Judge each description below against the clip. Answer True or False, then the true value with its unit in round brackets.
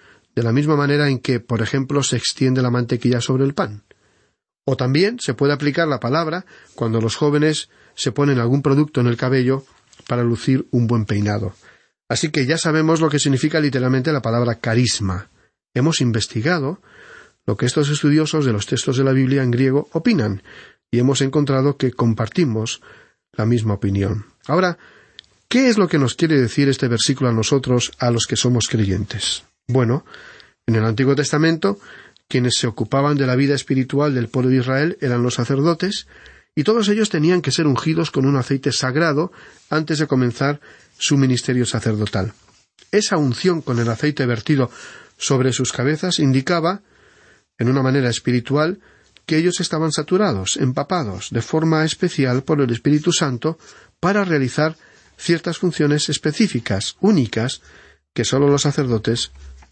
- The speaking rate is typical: True (160 wpm)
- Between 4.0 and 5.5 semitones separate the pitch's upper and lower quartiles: True (4.3 semitones)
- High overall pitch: False (135 Hz)